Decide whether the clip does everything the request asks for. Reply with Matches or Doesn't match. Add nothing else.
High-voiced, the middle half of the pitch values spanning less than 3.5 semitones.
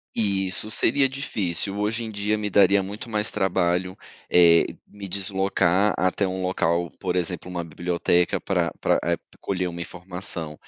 Doesn't match